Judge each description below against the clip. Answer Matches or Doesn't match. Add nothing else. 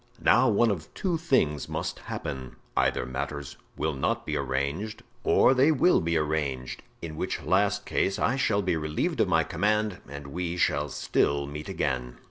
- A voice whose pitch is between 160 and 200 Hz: Doesn't match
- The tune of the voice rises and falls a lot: Matches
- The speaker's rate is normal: Matches